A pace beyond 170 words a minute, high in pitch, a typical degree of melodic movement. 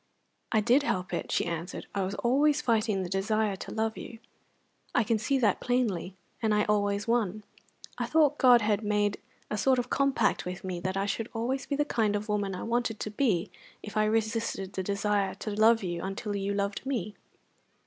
Yes: average, 200 wpm; high, 215 Hz; average, 3.0 semitones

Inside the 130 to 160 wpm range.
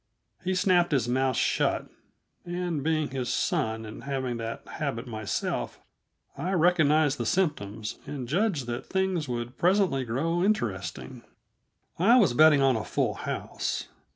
Yes: average, 140 wpm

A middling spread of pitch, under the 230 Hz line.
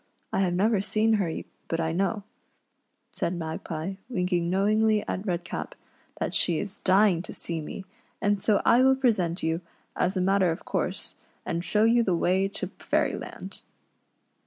Yes: average, 3.4 semitones; high, 190 Hz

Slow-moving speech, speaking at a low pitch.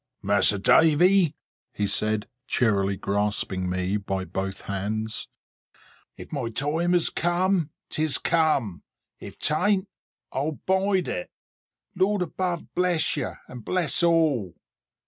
No: slow, 115 wpm; medium, 145 Hz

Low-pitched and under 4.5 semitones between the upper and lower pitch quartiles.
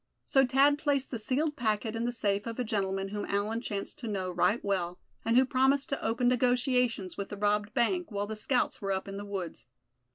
No: high, 225 Hz; average, 4.0 semitones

